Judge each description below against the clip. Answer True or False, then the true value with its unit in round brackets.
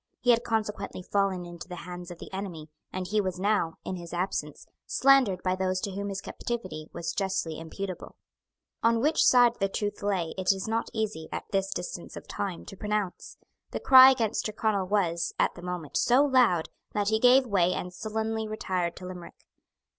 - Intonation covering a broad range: False (3.5 semitones)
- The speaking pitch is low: False (195 Hz)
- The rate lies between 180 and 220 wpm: True (190 wpm)